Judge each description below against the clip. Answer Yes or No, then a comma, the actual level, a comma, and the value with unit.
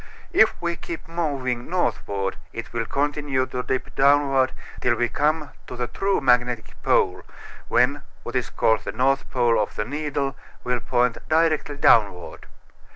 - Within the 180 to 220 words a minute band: No, average, 155 wpm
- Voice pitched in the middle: No, low, 130 Hz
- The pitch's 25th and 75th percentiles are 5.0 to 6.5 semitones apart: No, average, 3.4 semitones